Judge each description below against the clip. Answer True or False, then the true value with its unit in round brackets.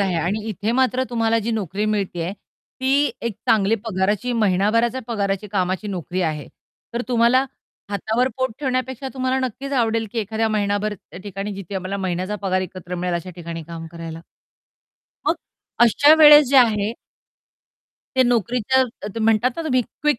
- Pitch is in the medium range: False (215 Hz)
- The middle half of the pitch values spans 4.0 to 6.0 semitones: True (4.8 semitones)